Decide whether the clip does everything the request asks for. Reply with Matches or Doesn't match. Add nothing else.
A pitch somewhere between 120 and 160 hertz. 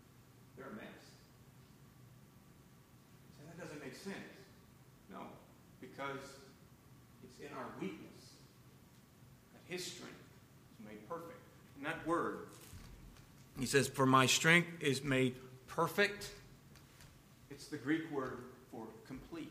Matches